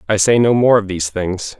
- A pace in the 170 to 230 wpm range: No, fast, 265 wpm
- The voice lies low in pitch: Yes, low, 105 Hz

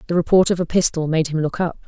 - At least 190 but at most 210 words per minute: No, fast, 290 wpm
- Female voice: Yes, female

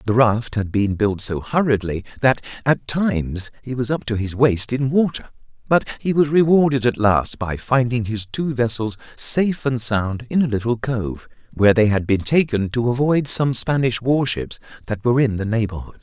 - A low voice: Yes, low, 120 Hz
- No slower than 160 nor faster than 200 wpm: Yes, average, 190 wpm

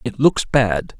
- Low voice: Yes, low, 130 Hz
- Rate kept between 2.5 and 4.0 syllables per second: Yes, 3.4 syllables/s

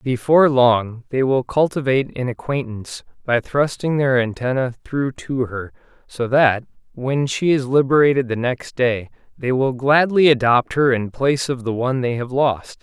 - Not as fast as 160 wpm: No, average, 170 wpm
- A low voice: Yes, low, 130 Hz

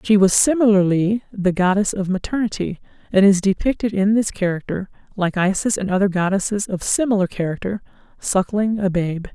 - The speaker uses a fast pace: No, average, 155 wpm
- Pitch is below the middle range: No, high, 195 Hz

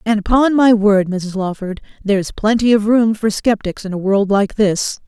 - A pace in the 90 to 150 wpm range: No, average, 200 wpm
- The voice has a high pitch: Yes, high, 210 Hz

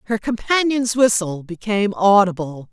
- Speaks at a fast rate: No, slow, 110 wpm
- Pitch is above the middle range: Yes, high, 210 Hz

